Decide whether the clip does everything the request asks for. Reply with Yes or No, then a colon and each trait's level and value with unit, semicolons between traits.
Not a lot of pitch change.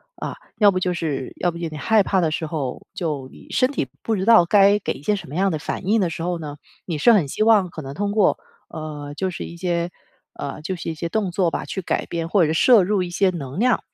No: average, 4.2 semitones